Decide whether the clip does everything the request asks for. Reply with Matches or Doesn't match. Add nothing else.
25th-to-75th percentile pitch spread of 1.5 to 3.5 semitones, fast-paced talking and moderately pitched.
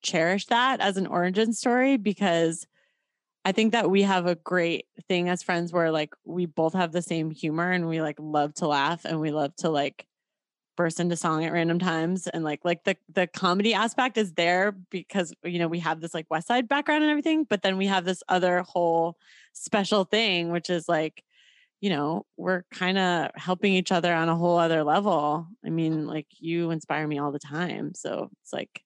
Matches